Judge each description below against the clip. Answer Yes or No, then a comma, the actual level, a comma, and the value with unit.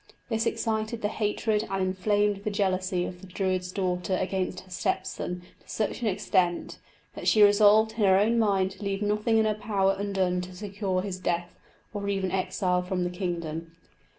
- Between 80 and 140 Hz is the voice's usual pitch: No, high, 195 Hz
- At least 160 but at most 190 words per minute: Yes, average, 185 wpm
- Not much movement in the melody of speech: Yes, narrow, 2.3 semitones